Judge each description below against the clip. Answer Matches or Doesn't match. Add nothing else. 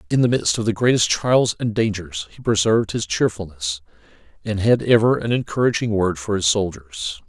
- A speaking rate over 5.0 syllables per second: Matches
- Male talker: Matches